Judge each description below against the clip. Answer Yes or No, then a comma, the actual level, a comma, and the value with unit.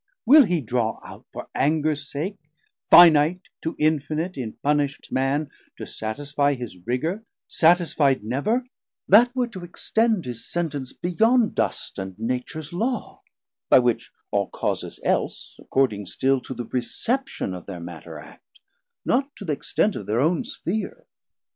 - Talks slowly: No, average, 145 wpm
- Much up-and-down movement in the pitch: Yes, wide, 6.9 semitones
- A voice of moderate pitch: Yes, medium, 150 Hz